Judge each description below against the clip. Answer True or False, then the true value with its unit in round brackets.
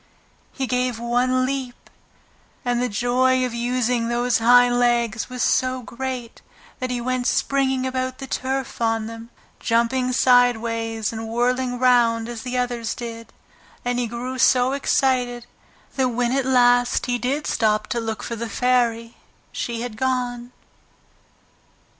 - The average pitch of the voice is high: True (245 Hz)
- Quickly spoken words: False (145 wpm)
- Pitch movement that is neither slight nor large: False (1.5 semitones)